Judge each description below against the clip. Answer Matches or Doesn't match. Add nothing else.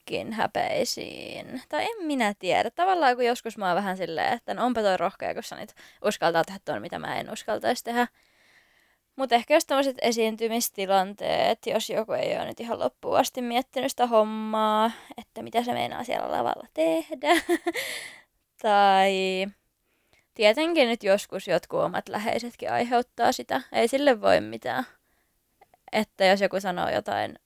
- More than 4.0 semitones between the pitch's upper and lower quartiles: Matches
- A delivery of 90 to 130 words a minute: Doesn't match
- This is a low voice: Doesn't match